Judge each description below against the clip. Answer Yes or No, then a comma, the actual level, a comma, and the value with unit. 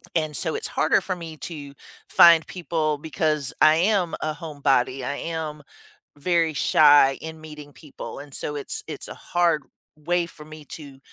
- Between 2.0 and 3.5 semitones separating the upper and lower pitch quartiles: Yes, narrow, 2.4 semitones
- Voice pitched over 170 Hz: No, medium, 155 Hz